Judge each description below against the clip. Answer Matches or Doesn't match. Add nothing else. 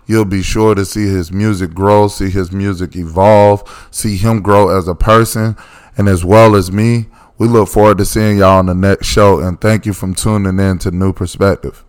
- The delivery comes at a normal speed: Doesn't match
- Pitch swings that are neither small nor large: Doesn't match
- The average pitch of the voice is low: Matches